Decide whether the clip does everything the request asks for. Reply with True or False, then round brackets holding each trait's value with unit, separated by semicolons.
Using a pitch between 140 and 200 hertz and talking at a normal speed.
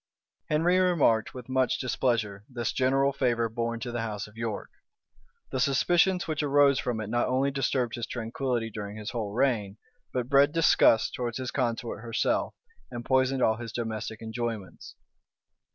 False (120 Hz; 160 wpm)